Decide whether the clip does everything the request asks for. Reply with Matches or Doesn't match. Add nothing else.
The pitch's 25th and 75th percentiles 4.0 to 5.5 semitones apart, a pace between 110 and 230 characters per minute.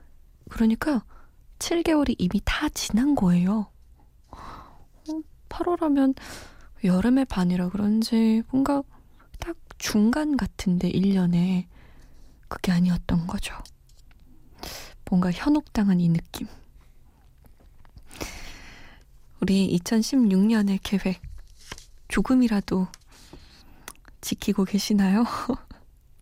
Matches